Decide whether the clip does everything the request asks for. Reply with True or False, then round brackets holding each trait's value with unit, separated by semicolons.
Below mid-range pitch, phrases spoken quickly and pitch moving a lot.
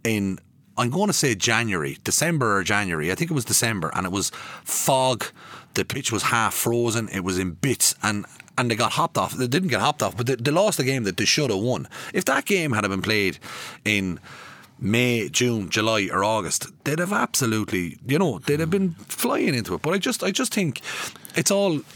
True (115 Hz; 215 wpm; 6.1 semitones)